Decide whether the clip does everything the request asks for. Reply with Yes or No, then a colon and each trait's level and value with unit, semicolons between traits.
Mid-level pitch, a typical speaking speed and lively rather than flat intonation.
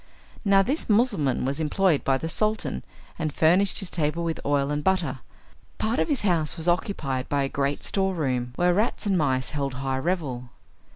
Yes: medium, 160 Hz; average, 180 wpm; wide, 5.7 semitones